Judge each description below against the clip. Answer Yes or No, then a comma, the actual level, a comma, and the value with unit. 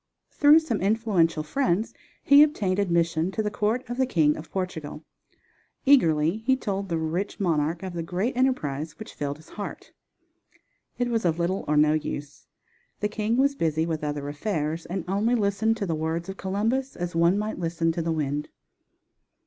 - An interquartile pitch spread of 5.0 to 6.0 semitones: Yes, wide, 5.4 semitones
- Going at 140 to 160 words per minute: No, average, 180 wpm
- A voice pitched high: No, medium, 180 Hz